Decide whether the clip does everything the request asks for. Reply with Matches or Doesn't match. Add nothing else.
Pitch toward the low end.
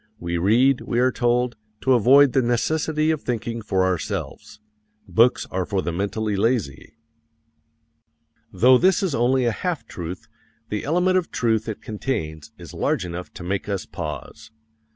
Matches